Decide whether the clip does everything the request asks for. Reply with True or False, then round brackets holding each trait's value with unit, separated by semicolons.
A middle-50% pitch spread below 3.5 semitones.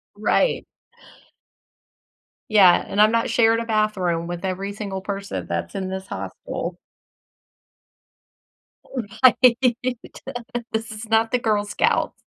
True (2.8 semitones)